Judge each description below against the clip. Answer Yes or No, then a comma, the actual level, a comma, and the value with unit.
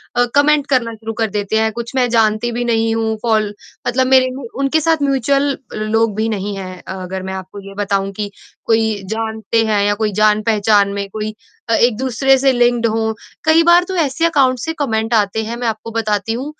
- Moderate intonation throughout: Yes, average, 3.3 semitones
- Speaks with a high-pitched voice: Yes, high, 225 Hz